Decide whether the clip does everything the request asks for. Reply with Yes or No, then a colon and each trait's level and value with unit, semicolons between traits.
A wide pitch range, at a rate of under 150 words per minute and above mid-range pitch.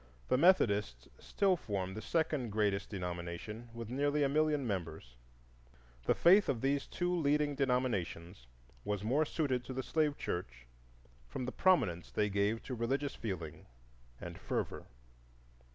No: wide, 6.9 semitones; average, 140 wpm; low, 120 Hz